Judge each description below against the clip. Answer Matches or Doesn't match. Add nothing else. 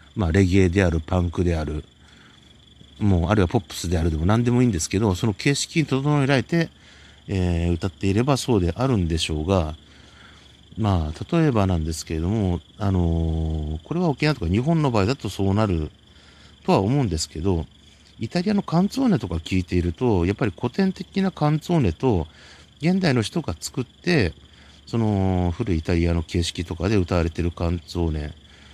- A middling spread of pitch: Doesn't match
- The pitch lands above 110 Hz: Doesn't match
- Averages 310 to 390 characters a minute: Matches